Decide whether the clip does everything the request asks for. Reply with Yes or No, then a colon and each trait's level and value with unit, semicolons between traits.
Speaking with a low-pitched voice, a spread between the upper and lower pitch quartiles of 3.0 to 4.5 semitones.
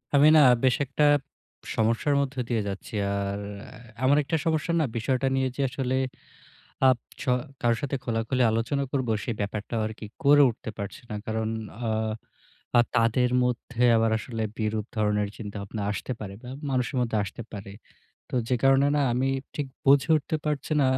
Yes: low, 125 Hz; average, 3.5 semitones